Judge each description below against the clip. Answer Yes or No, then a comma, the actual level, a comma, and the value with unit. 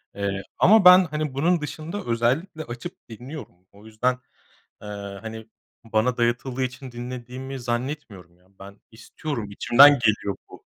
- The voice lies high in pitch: No, low, 120 Hz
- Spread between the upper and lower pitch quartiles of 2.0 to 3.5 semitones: No, average, 4.5 semitones